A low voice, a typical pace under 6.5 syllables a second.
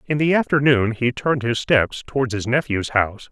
Yes: low, 125 Hz; 5.4 syllables/s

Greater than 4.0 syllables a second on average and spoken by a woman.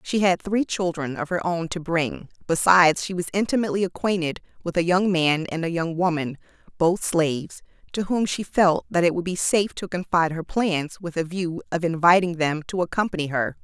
Yes: 5.4 syllables/s; female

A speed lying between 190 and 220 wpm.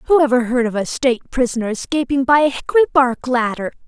Yes: average, 200 wpm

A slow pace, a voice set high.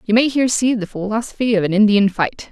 No: fast, 240 wpm; high, 215 Hz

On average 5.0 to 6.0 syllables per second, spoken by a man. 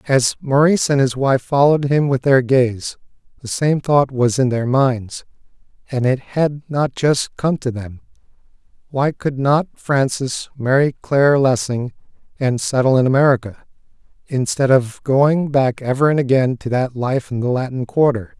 No: 4.5 syllables/s; male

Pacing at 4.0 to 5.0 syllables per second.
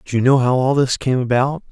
No: 5.8 syllables/s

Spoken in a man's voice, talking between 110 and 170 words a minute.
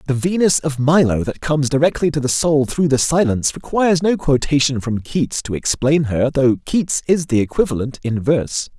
No: male; average, 190 wpm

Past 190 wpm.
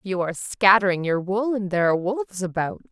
Yes: fast, 205 wpm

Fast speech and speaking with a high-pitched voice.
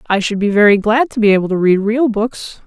Yes: fast, 270 wpm; high, 215 Hz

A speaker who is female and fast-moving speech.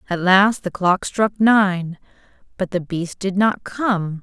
No: female; average, 170 wpm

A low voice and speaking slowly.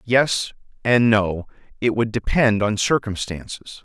Yes: low, 110 Hz; slow, 110 wpm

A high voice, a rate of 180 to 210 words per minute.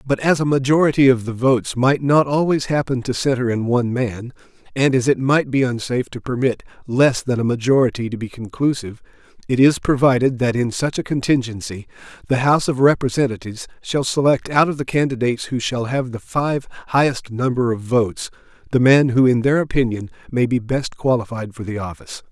No: low, 125 Hz; average, 190 wpm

